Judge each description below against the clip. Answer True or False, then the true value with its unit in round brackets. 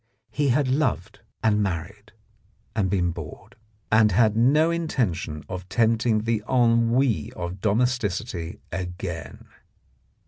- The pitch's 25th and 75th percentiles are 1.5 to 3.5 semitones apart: False (4.7 semitones)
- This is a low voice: True (105 Hz)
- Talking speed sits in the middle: False (110 wpm)